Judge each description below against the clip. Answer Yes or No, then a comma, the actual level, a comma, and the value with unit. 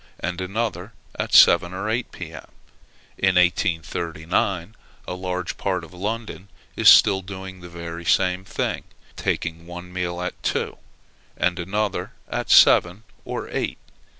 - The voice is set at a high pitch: No, very low, 90 Hz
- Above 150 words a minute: No, slow, 135 wpm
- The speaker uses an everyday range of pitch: No, narrow, 1.8 semitones